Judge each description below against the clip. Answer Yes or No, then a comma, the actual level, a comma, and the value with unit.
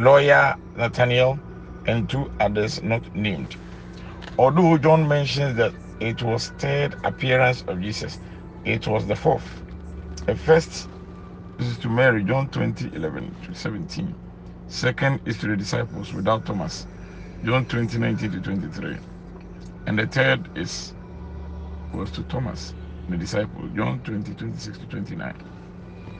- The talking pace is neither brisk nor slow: No, slow, 130 wpm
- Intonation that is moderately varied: No, wide, 6.1 semitones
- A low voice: Yes, very low, 95 Hz